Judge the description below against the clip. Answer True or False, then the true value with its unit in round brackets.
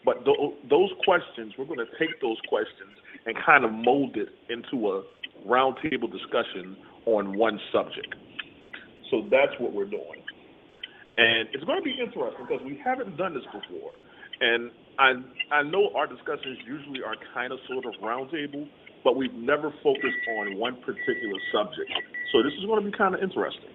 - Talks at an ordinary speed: True (170 wpm)